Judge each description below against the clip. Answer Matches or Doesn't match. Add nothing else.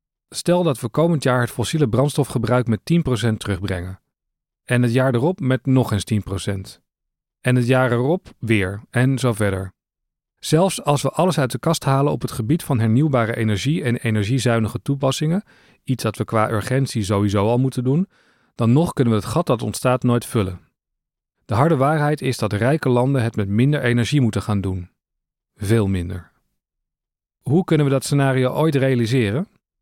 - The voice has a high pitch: Doesn't match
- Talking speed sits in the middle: Matches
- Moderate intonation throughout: Matches